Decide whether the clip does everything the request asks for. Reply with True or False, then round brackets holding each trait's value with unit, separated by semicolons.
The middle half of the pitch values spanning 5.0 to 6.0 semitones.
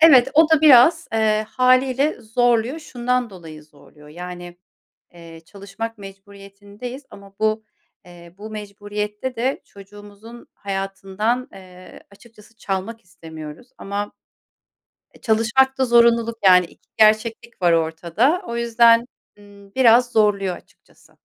False (3.6 semitones)